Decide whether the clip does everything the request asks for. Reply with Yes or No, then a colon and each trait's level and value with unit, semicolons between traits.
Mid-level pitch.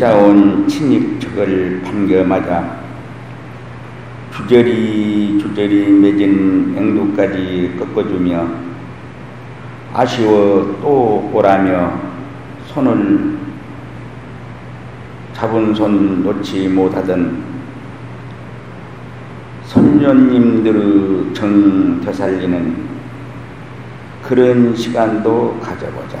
No: low, 105 Hz